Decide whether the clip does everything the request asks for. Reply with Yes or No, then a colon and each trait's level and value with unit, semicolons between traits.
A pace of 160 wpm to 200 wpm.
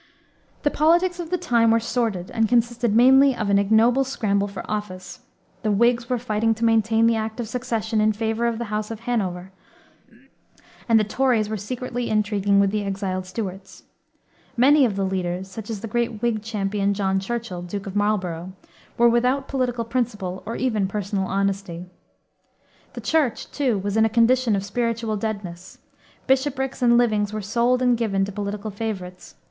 Yes: average, 175 wpm